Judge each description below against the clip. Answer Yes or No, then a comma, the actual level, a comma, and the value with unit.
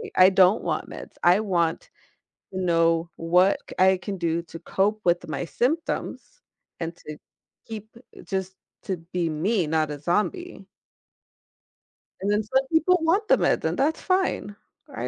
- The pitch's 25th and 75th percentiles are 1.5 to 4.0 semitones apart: No, average, 4.9 semitones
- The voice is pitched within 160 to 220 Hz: Yes, high, 190 Hz